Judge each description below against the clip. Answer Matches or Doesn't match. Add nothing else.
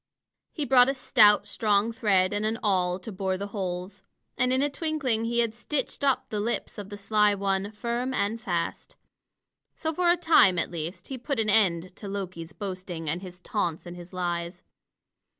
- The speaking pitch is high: Matches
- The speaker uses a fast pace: Doesn't match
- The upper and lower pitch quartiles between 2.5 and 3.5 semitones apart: Doesn't match